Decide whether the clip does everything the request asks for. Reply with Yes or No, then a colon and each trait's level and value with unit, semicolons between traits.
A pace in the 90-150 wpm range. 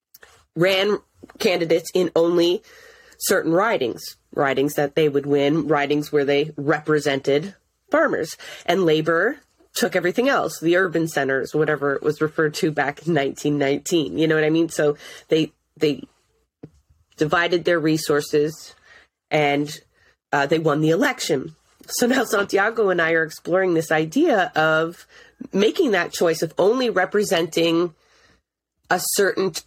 Yes: average, 140 wpm